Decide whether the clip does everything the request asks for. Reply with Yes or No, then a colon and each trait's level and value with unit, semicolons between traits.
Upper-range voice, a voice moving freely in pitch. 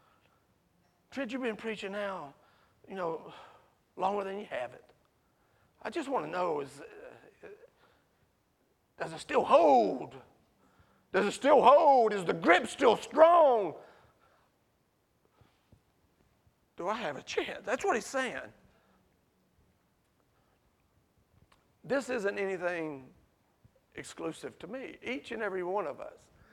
Yes: high, 225 Hz; wide, 7.0 semitones